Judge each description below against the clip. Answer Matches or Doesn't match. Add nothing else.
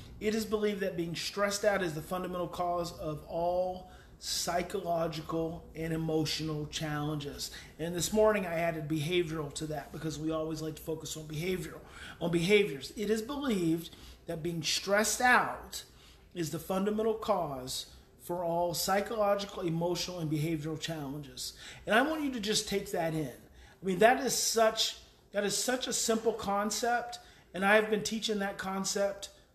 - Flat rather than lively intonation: Doesn't match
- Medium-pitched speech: Matches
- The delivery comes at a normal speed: Matches